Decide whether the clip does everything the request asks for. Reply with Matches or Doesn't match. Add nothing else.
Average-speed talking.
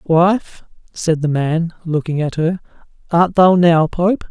Matches